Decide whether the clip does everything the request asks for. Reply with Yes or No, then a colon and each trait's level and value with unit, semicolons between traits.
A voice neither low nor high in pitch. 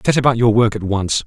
No: low, 115 Hz